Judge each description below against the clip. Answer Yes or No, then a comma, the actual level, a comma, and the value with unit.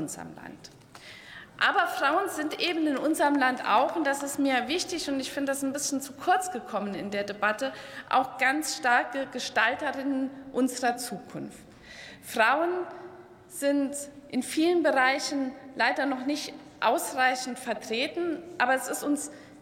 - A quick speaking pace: No, average, 145 wpm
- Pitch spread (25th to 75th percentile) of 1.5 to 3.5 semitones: Yes, average, 2.8 semitones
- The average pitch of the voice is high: Yes, very high, 275 Hz